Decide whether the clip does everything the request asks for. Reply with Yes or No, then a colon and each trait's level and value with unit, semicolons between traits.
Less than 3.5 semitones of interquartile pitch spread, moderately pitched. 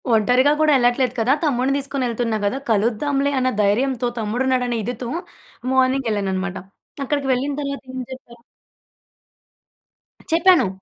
No: average, 2.9 semitones; very high, 255 Hz